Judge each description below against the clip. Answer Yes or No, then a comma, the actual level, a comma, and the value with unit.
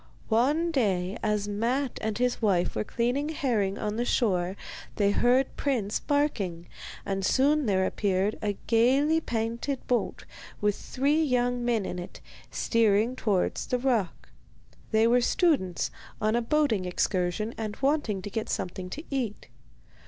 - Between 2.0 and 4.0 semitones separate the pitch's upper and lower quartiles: No, average, 4.5 semitones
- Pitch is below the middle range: No, high, 225 Hz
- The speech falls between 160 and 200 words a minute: No, average, 145 wpm